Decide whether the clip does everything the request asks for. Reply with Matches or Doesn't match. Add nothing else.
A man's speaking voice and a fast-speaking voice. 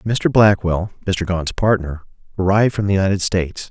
Doesn't match